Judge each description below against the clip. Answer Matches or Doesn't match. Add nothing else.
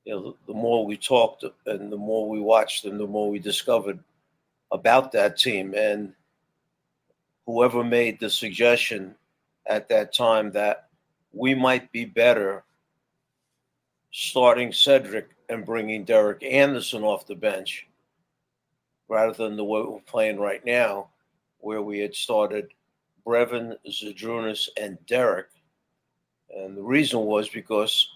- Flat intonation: Matches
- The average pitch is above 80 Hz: Matches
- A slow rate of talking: Matches